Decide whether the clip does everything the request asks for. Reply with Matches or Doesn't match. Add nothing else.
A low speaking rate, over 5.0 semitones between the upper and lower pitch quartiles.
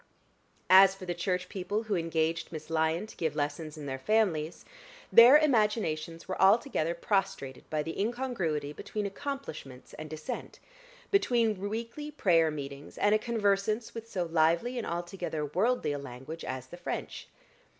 Doesn't match